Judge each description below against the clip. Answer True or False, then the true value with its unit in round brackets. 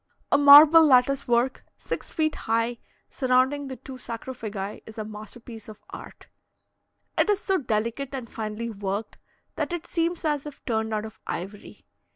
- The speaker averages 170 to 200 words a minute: False (160 wpm)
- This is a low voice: False (245 Hz)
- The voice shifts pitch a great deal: False (4.6 semitones)